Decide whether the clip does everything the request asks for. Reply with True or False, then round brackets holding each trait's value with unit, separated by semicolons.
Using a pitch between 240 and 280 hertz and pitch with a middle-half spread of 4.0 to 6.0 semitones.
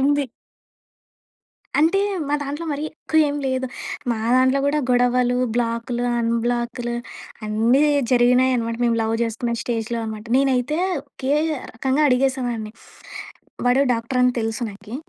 False (245 Hz; 2.5 semitones)